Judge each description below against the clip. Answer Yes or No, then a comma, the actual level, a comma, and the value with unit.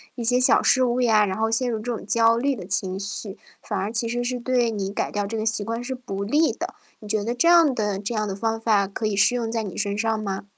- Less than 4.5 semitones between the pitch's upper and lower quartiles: Yes, average, 2.9 semitones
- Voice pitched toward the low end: No, high, 225 Hz